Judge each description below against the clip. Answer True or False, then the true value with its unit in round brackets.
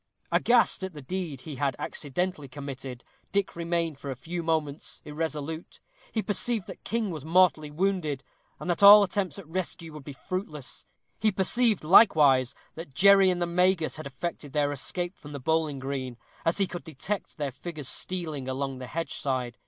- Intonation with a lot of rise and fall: False (4.6 semitones)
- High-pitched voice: False (160 Hz)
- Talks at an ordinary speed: True (175 wpm)